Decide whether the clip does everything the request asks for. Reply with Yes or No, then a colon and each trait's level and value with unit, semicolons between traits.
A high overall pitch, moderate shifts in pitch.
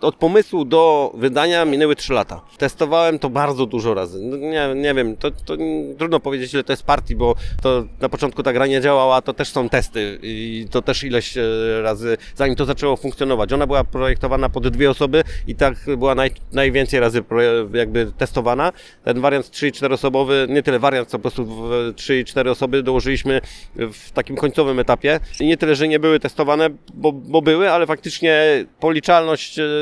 No: low, 135 Hz; average, 3.1 semitones